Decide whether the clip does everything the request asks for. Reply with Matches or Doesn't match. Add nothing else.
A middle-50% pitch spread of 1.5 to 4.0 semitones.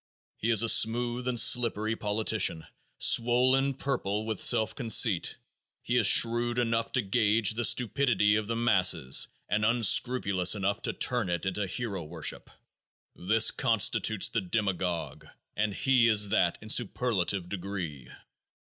Matches